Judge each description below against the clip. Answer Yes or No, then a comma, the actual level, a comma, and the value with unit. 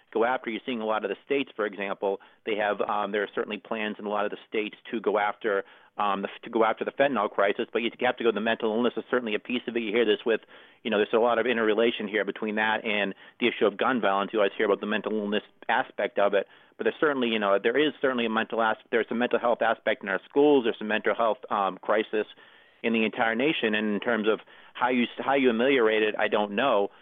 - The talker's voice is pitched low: Yes, low, 115 Hz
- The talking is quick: Yes, fast, 265 wpm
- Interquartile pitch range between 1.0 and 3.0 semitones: Yes, narrow, 2.6 semitones